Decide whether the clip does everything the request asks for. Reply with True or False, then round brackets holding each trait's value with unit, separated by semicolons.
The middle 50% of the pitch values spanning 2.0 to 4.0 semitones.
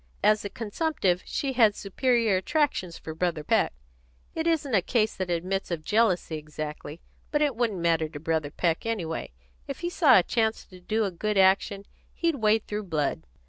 False (5.3 semitones)